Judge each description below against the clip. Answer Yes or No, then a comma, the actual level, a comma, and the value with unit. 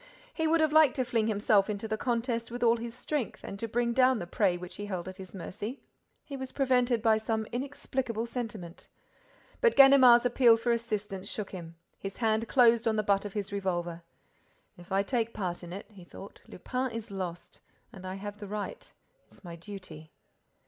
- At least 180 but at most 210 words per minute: Yes, average, 195 wpm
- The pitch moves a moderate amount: Yes, average, 3.8 semitones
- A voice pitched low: No, high, 220 Hz